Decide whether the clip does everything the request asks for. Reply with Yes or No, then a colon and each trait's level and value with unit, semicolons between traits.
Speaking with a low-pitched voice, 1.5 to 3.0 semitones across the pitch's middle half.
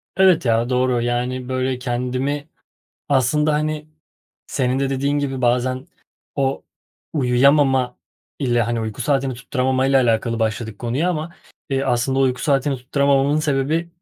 Yes: low, 130 Hz; narrow, 2.4 semitones